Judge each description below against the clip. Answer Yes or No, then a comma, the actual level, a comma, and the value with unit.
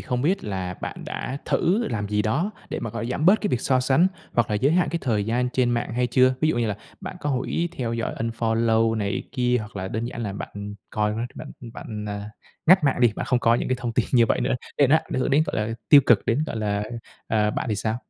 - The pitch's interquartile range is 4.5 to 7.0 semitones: No, average, 3.3 semitones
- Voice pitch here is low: Yes, low, 120 Hz